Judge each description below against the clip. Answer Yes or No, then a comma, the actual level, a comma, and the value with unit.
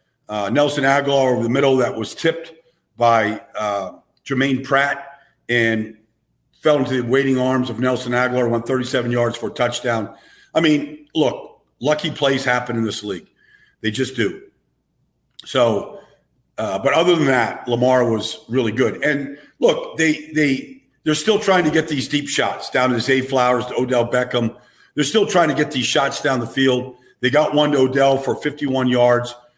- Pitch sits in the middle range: No, low, 130 Hz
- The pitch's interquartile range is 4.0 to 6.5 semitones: No, average, 3.3 semitones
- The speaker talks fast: No, average, 175 wpm